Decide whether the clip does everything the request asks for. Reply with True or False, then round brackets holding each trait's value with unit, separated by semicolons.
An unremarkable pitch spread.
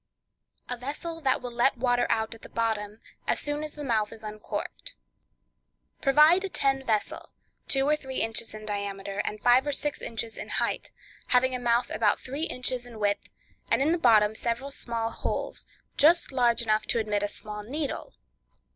True (4.0 semitones)